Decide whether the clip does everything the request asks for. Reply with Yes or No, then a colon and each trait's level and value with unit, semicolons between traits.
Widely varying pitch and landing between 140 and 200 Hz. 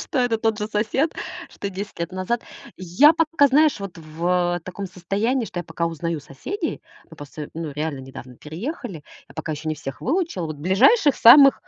Yes: wide, 7.5 semitones; medium, 185 Hz